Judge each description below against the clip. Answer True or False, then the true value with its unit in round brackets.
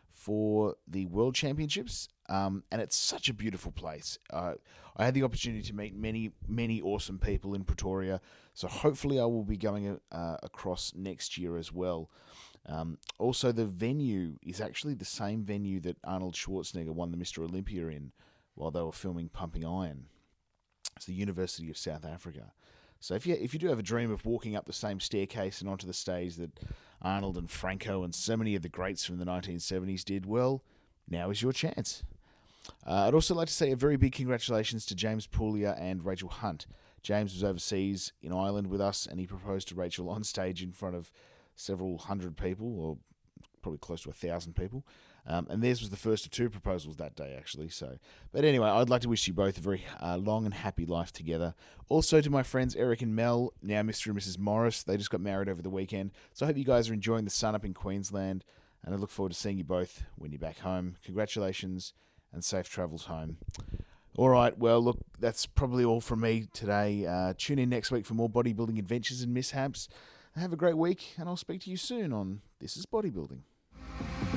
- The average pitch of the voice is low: True (100 Hz)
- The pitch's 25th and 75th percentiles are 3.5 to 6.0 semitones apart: True (4.1 semitones)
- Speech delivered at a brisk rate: True (210 wpm)